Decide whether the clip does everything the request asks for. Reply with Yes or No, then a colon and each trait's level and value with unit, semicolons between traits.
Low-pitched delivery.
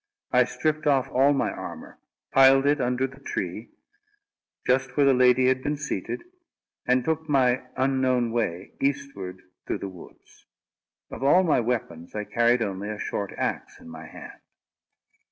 Yes: low, 130 Hz